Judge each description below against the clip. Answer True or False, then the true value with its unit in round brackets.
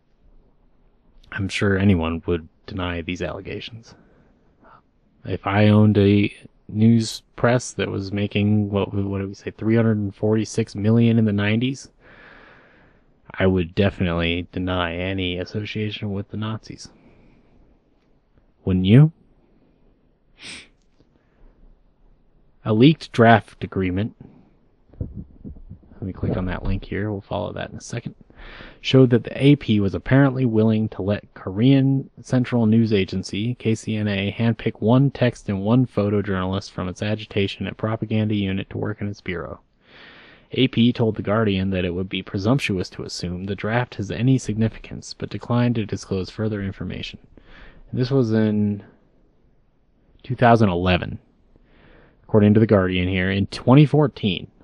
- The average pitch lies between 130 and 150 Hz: False (105 Hz)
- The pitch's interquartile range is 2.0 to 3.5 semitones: True (3.0 semitones)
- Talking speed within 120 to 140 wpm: True (135 wpm)